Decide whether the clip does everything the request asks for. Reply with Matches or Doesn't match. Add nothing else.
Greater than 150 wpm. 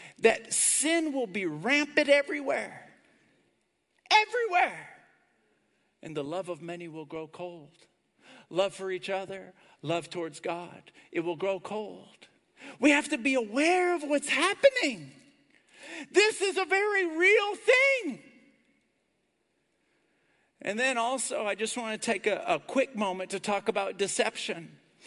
Doesn't match